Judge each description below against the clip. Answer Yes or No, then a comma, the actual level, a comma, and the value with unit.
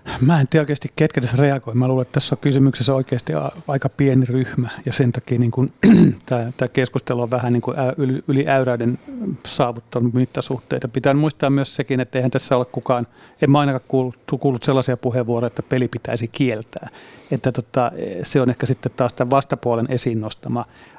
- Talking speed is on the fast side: Yes, fast, 170 wpm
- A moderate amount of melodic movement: No, narrow, 2.0 semitones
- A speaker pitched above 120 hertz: Yes, low, 130 Hz